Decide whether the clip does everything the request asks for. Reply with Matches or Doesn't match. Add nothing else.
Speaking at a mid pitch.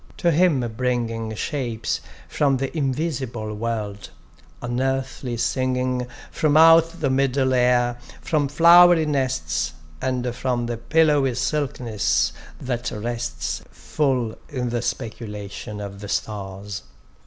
Doesn't match